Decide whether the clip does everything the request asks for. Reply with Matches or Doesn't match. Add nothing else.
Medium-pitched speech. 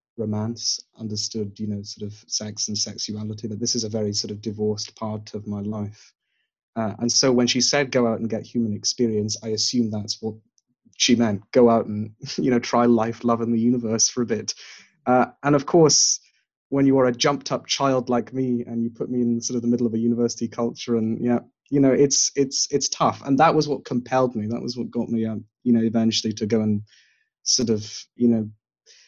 Doesn't match